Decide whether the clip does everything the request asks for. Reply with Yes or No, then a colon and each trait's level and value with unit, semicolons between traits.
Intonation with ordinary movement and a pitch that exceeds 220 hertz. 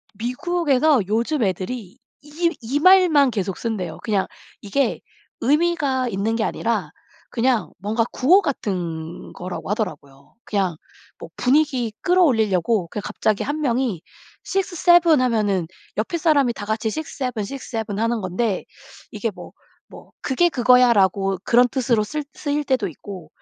No: wide, 5.9 semitones; high, 235 Hz